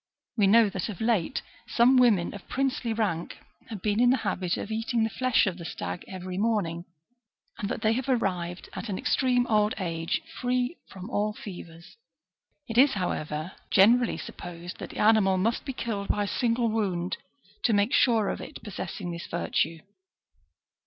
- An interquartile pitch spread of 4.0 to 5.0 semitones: Yes, average, 4.3 semitones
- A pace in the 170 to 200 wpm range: Yes, average, 175 wpm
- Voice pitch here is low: No, high, 210 Hz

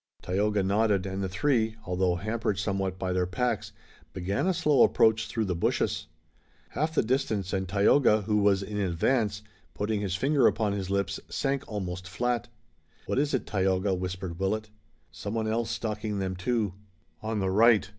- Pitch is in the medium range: No, low, 105 Hz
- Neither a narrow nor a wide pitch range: Yes, average, 3.1 semitones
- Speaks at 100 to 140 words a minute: No, average, 165 wpm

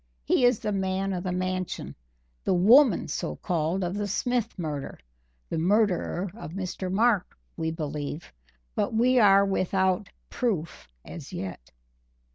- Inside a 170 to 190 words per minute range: No, average, 140 wpm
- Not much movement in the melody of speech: No, average, 3.5 semitones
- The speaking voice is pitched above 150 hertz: Yes, medium, 185 Hz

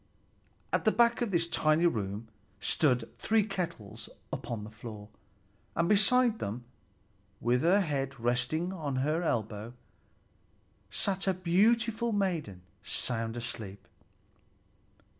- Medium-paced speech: No, slow, 115 wpm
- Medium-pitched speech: Yes, medium, 155 Hz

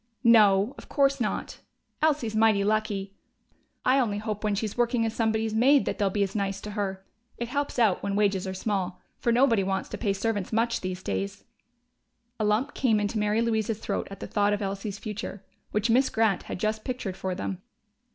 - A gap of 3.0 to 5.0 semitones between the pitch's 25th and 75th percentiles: No, narrow, 2.5 semitones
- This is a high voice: Yes, high, 215 Hz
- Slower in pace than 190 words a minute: No, average, 200 wpm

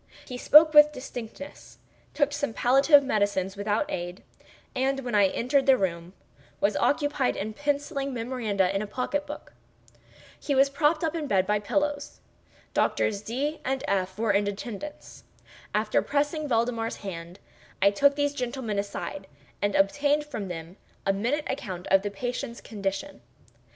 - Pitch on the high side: Yes, high, 240 Hz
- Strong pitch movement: Yes, wide, 6.1 semitones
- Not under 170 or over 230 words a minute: No, average, 150 wpm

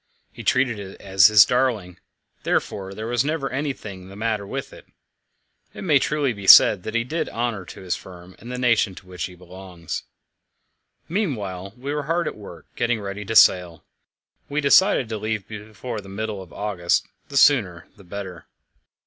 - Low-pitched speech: Yes, low, 105 Hz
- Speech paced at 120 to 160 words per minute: No, average, 180 wpm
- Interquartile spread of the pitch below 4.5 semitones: No, average, 4.9 semitones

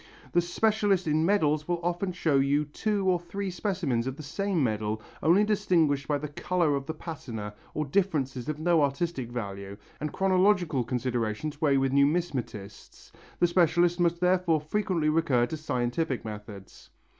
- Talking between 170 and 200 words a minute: No, average, 155 wpm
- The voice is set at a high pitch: No, medium, 155 Hz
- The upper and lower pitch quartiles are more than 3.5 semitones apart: Yes, average, 5.0 semitones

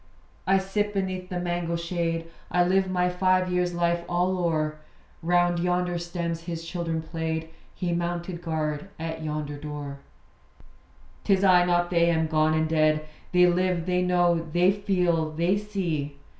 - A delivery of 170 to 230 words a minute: No, average, 155 wpm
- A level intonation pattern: Yes, narrow, 1.8 semitones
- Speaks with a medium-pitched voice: Yes, medium, 175 Hz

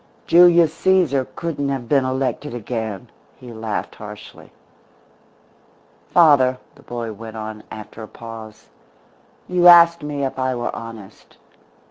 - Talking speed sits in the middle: No, slow, 125 wpm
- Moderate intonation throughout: Yes, average, 4.9 semitones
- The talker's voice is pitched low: Yes, low, 130 Hz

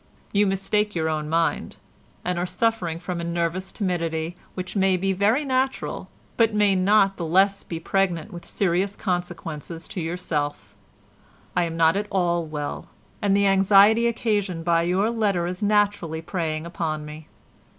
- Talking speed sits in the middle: Yes, average, 160 wpm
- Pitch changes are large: No, average, 3.2 semitones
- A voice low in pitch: No, medium, 180 Hz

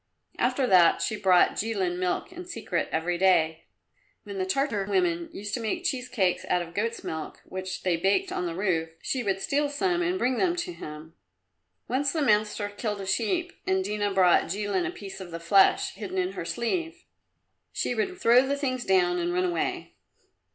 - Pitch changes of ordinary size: No, wide, 6.0 semitones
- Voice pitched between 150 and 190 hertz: No, high, 200 Hz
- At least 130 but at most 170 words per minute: No, average, 195 wpm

